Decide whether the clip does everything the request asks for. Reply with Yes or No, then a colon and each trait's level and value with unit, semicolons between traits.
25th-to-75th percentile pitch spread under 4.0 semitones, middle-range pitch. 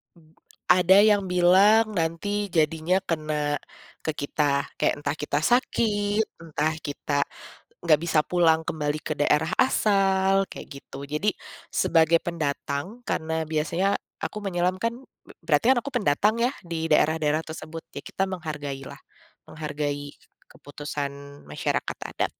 No: average, 4.4 semitones; medium, 160 Hz